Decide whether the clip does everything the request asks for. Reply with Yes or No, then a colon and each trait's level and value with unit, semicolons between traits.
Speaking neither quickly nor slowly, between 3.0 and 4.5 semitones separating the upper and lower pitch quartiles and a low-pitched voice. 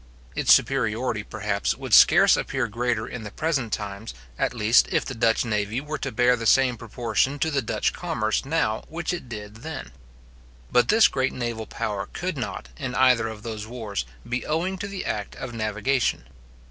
Yes: average, 185 wpm; average, 3.6 semitones; low, 120 Hz